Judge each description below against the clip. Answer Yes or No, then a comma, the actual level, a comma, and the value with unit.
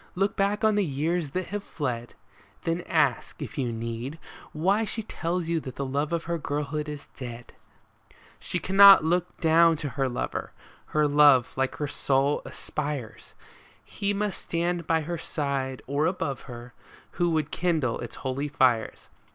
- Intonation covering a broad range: No, average, 4.4 semitones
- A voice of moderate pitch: Yes, medium, 150 Hz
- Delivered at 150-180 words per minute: Yes, average, 165 wpm